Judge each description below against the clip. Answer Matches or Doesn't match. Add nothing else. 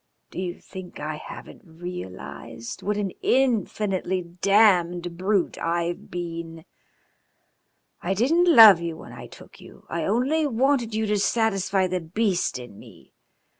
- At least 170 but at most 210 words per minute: Doesn't match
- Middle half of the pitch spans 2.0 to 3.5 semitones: Doesn't match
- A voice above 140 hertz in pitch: Matches